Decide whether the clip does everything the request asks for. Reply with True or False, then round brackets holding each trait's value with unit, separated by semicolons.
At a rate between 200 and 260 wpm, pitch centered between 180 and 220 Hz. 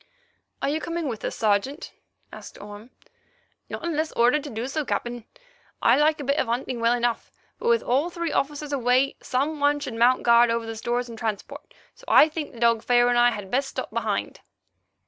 False (205 wpm; 250 Hz)